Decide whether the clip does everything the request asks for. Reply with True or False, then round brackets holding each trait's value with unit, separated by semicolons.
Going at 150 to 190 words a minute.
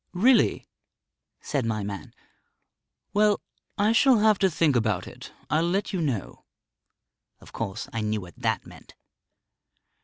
False (140 wpm)